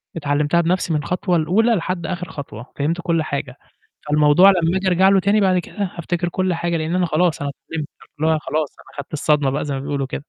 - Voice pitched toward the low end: No, medium, 165 Hz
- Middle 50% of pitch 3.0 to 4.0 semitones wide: Yes, average, 3.5 semitones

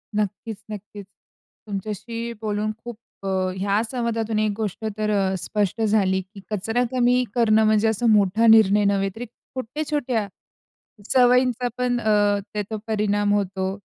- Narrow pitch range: Yes, narrow, 2.3 semitones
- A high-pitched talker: Yes, high, 215 Hz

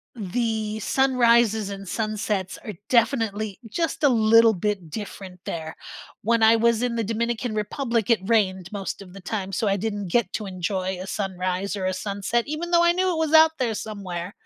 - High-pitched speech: Yes, high, 215 Hz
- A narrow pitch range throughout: No, average, 3.2 semitones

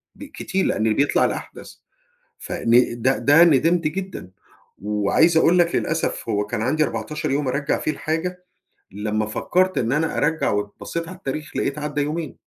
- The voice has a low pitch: No, medium, 150 Hz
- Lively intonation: Yes, wide, 6.2 semitones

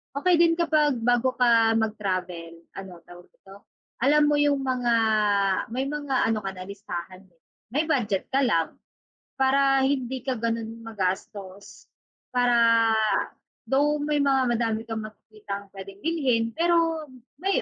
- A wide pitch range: Yes, wide, 5.8 semitones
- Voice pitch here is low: No, high, 235 Hz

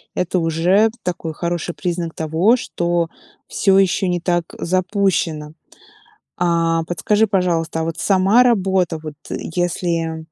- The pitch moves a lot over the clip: No, narrow, 2.5 semitones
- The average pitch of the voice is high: No, medium, 175 Hz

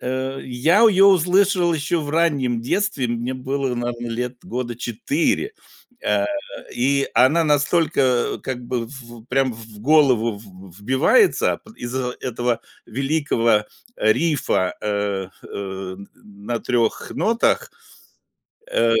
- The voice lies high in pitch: No, low, 125 Hz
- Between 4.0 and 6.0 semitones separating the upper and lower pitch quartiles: Yes, average, 4.6 semitones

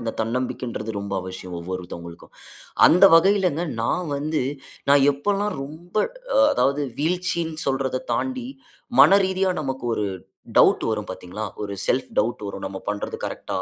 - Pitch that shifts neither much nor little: No, wide, 9.0 semitones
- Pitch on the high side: No, low, 135 Hz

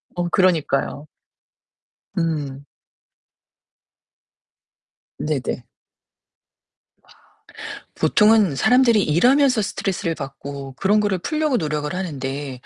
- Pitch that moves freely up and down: Yes, wide, 6.8 semitones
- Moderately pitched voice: Yes, medium, 165 Hz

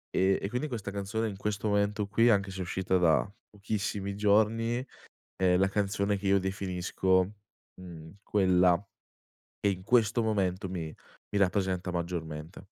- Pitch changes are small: Yes, narrow, 2.2 semitones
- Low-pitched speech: Yes, low, 100 Hz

